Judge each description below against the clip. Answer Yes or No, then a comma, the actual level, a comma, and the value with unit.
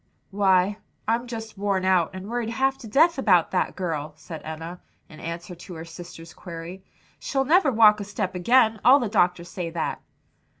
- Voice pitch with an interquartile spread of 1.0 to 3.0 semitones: No, average, 4.7 semitones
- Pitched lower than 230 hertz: Yes, high, 190 Hz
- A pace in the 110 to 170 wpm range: No, average, 180 wpm